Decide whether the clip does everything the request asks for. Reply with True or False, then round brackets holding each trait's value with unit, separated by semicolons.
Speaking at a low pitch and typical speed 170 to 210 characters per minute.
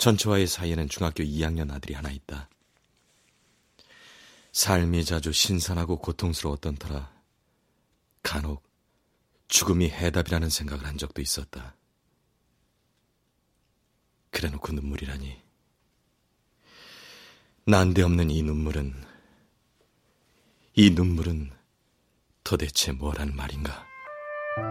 True (80 Hz; 205 characters per minute)